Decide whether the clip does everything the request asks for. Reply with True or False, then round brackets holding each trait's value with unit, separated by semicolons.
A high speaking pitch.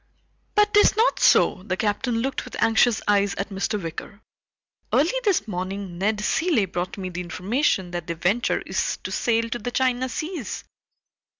True (210 Hz)